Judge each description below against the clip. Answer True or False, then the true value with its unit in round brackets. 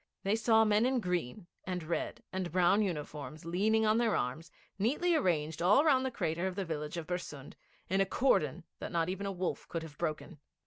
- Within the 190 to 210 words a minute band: True (200 wpm)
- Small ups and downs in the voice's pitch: False (5.0 semitones)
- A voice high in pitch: False (180 Hz)